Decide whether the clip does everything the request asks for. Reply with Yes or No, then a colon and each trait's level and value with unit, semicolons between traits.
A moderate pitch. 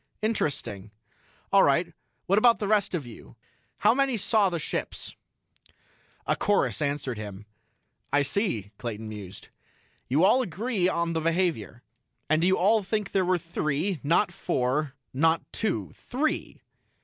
Yes: medium, 170 Hz